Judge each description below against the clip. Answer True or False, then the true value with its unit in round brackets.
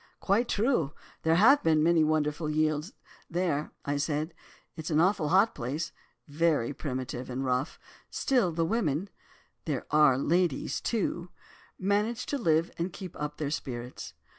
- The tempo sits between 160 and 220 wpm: False (135 wpm)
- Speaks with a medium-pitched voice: True (160 Hz)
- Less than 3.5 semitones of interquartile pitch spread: False (4.0 semitones)